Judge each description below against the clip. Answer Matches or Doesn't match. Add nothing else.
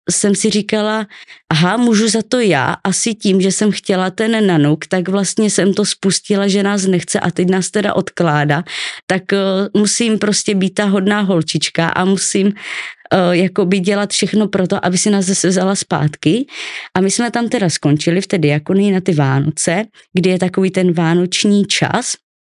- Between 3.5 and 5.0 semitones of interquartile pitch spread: Doesn't match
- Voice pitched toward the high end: Matches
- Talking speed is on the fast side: Matches